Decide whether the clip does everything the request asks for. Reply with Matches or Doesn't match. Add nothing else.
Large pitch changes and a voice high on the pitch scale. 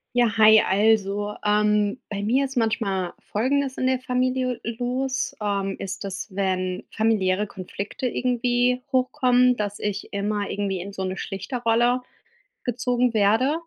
Doesn't match